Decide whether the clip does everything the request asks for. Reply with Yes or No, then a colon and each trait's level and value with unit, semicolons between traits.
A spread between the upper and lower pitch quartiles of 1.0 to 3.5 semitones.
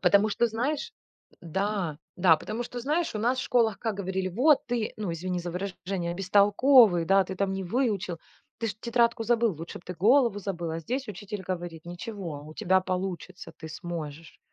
No: average, 4.5 semitones